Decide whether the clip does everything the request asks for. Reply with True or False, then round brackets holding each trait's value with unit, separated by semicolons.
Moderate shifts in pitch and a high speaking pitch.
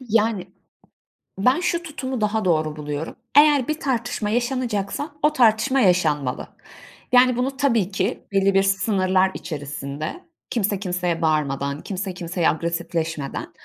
False (7.0 semitones; 195 Hz)